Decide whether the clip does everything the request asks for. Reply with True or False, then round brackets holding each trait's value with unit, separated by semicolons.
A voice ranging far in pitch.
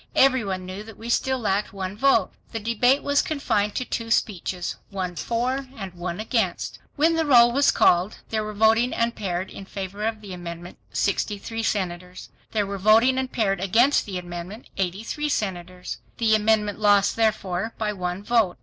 False (3.7 semitones)